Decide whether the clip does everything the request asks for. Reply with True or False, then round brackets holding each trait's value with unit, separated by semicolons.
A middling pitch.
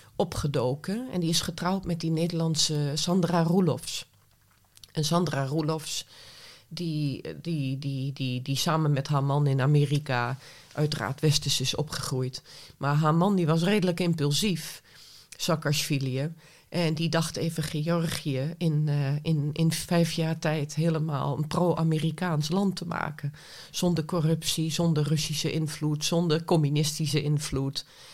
True (155 Hz)